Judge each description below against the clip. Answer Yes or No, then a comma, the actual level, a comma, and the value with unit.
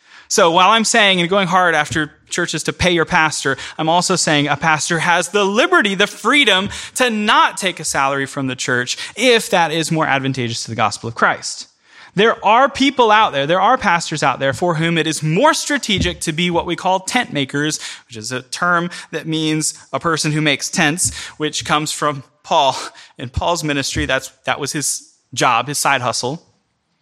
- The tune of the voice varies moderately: Yes, average, 4.3 semitones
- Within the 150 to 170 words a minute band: No, average, 200 wpm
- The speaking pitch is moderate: Yes, medium, 160 Hz